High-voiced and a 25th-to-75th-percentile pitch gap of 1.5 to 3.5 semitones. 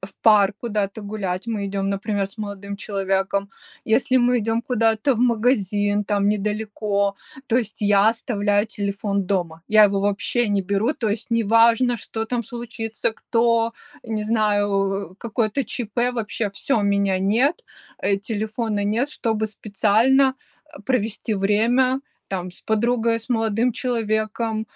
Yes: high, 215 Hz; narrow, 2.4 semitones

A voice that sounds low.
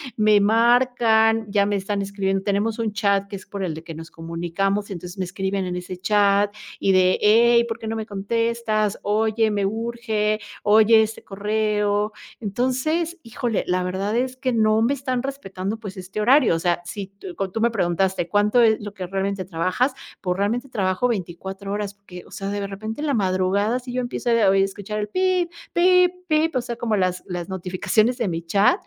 No: high, 210 Hz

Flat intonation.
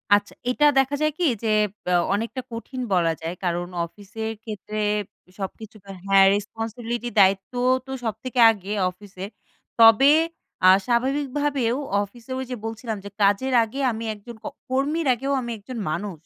No: average, 4.2 semitones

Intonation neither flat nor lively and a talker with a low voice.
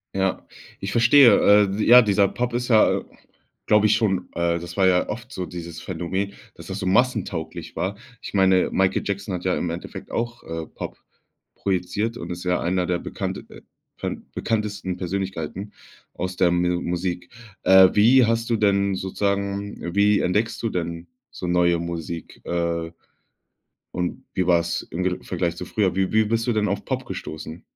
Yes: average, 3.1 semitones; very low, 95 Hz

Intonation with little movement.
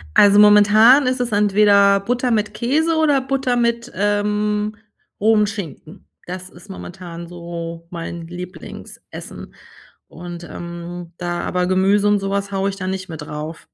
No: average, 3.3 semitones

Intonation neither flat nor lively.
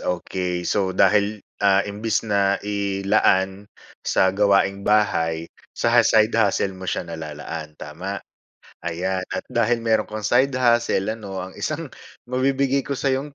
Yes: average, 3.3 semitones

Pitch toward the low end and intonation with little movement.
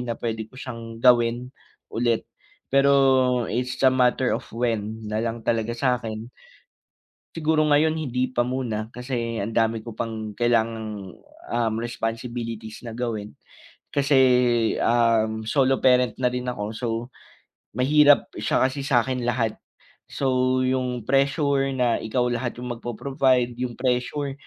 Yes: low, 120 Hz; narrow, 2.2 semitones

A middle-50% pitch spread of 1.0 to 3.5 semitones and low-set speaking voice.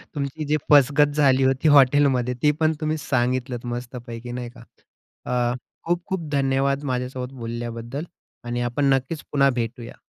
Yes: average, 2.9 semitones; low, 130 Hz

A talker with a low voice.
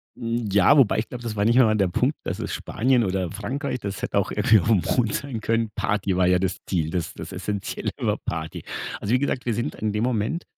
Yes: low, 110 Hz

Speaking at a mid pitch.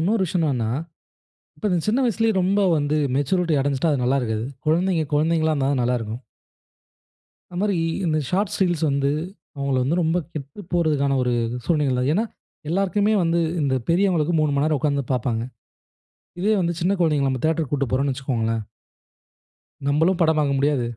Yes: medium, 155 Hz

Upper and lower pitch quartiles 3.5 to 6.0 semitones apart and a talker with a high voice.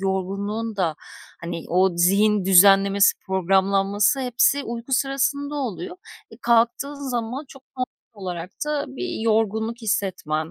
Yes: average, 4.1 semitones; high, 205 Hz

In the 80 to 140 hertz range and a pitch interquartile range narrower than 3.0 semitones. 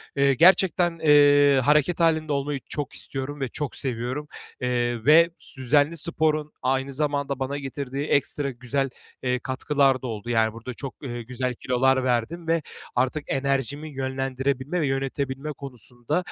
Yes: low, 135 Hz; narrow, 2.5 semitones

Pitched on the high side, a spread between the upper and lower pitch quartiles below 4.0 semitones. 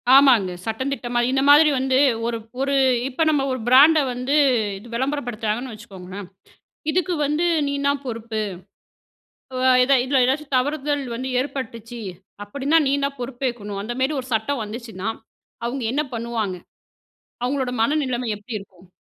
Yes: very high, 255 Hz; average, 3.5 semitones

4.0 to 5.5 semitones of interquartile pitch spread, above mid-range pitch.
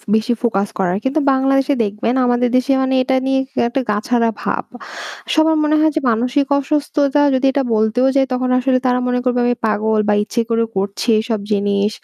No: average, 3.5 semitones; very high, 250 Hz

